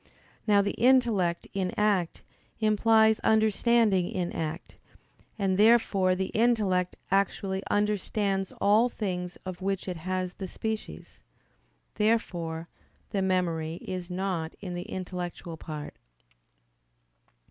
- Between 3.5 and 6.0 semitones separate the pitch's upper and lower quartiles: No, average, 3.0 semitones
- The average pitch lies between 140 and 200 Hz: Yes, high, 190 Hz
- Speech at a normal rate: No, slow, 110 wpm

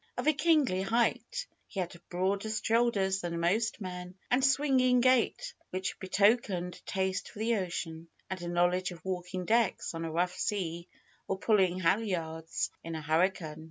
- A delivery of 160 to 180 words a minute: Yes, average, 165 wpm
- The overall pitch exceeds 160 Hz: Yes, high, 190 Hz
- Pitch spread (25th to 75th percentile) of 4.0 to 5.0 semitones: Yes, average, 4.4 semitones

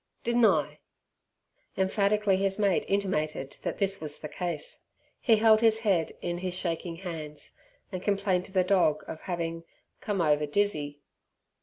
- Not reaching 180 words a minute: Yes, average, 150 wpm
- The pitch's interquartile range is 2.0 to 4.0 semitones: Yes, average, 3.6 semitones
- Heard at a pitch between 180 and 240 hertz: Yes, medium, 185 Hz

